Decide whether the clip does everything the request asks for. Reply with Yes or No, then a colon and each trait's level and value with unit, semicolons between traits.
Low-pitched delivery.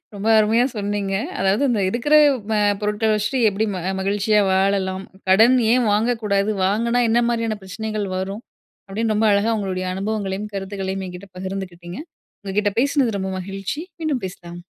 No: high, 205 Hz